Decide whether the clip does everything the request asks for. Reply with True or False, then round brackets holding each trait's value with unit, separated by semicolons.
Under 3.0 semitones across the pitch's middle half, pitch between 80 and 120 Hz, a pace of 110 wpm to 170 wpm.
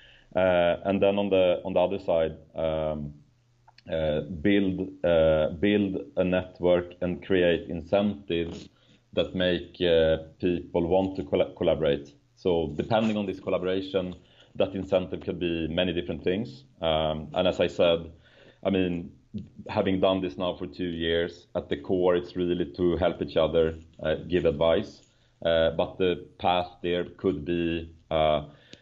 True (2.4 semitones; 90 Hz; 150 wpm)